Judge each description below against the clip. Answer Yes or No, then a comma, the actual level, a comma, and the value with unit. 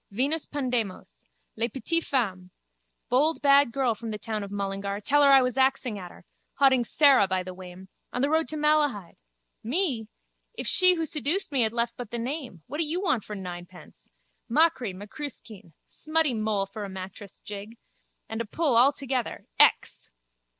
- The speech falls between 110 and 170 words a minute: No, average, 180 wpm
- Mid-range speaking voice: No, high, 240 Hz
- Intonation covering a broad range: Yes, wide, 6.0 semitones